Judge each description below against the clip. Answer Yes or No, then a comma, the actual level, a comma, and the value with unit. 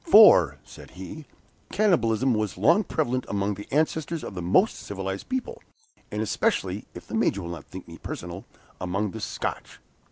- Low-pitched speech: Yes, low, 105 Hz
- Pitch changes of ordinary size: No, wide, 8.7 semitones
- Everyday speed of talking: Yes, average, 165 wpm